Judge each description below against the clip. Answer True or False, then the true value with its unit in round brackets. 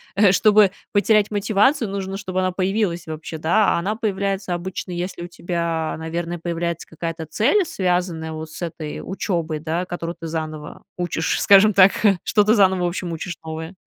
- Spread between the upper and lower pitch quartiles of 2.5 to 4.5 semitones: True (3.2 semitones)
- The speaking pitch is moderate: True (180 Hz)